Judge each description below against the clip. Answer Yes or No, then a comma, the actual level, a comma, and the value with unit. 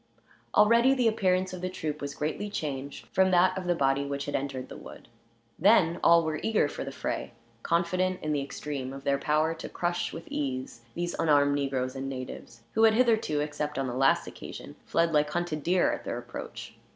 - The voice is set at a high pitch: No, medium, 155 Hz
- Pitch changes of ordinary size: Yes, average, 4.6 semitones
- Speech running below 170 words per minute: No, average, 200 wpm